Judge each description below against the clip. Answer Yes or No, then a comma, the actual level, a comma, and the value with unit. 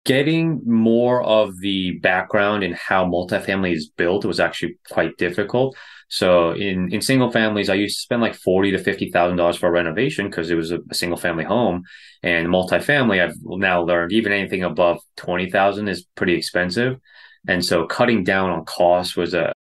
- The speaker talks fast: No, average, 185 wpm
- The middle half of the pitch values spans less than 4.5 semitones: Yes, average, 3.5 semitones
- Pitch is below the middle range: Yes, very low, 95 Hz